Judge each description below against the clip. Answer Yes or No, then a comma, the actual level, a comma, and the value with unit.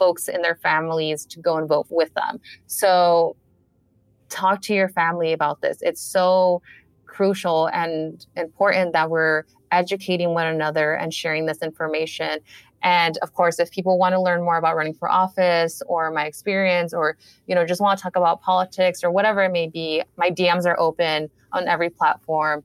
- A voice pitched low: No, medium, 170 Hz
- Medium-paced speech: Yes, average, 180 wpm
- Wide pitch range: No, narrow, 2.4 semitones